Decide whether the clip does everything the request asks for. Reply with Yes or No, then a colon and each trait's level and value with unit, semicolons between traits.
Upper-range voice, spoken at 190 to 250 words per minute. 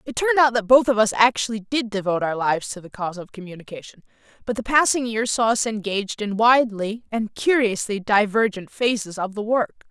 Yes: high, 220 Hz; average, 200 wpm